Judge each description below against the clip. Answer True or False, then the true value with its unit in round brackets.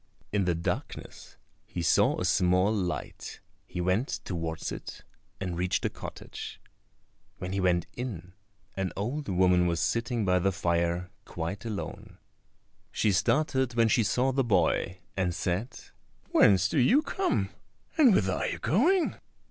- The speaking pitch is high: False (95 Hz)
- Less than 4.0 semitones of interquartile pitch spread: False (5.0 semitones)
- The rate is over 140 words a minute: True (150 wpm)